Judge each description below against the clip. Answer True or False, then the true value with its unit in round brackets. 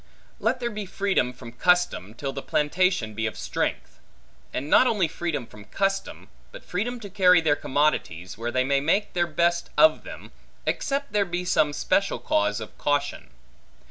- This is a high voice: False (170 Hz)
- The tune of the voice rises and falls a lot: True (6.3 semitones)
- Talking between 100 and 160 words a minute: False (175 wpm)